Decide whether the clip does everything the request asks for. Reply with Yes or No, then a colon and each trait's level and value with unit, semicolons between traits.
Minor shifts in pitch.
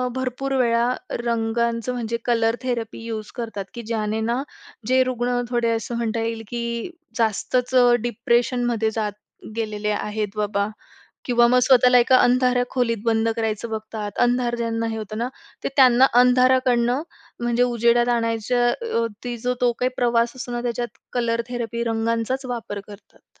Yes: narrow, 1.6 semitones